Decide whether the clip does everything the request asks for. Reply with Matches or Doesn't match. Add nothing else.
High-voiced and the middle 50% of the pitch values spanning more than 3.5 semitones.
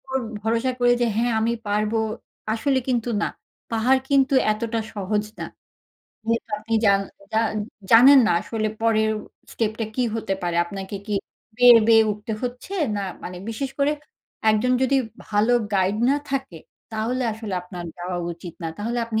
Doesn't match